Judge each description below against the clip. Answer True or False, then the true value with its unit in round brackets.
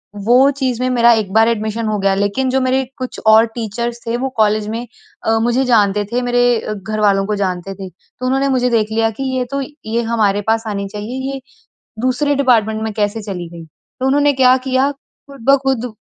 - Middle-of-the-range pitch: False (230 Hz)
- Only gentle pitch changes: False (3.5 semitones)